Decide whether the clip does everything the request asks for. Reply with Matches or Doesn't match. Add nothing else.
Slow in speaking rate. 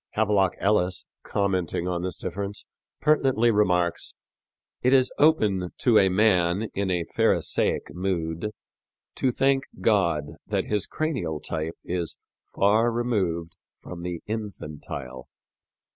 Matches